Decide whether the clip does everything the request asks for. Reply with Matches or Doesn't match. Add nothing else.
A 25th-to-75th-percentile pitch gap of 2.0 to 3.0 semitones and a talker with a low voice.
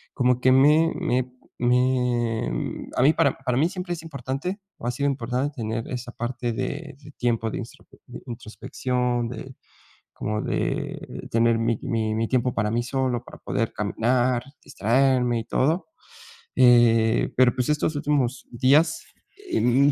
Matches